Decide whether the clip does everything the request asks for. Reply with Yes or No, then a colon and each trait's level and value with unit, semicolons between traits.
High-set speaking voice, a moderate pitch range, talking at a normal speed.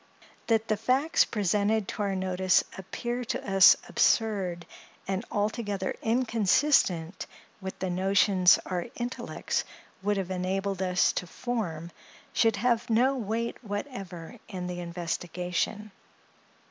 No: high, 200 Hz; average, 3.6 semitones; slow, 120 wpm